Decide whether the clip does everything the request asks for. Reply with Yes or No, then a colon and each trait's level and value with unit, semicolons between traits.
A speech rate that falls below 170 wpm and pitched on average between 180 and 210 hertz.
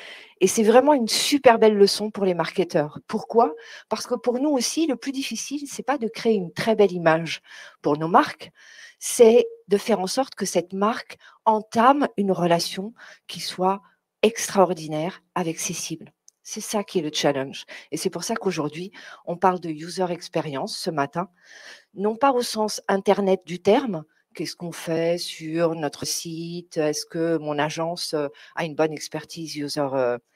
No: average, 175 wpm; medium, 185 Hz